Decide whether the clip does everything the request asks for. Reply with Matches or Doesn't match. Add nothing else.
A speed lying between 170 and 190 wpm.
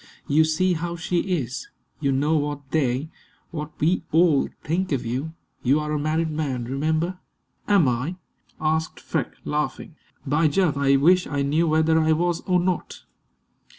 Doesn't match